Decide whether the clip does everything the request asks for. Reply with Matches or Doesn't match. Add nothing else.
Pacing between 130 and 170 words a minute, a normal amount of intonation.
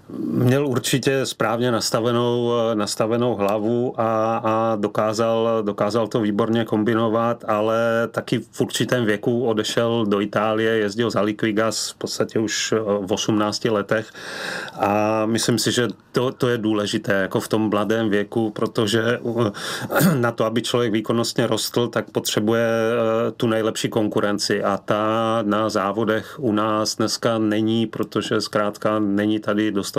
Doesn't match